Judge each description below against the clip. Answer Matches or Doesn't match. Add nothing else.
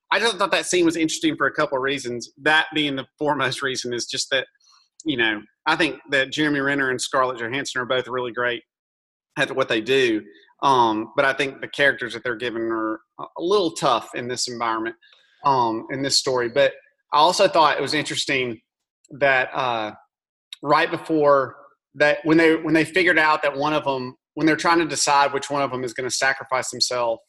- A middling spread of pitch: Matches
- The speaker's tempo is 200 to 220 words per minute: Matches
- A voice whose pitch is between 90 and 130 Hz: Doesn't match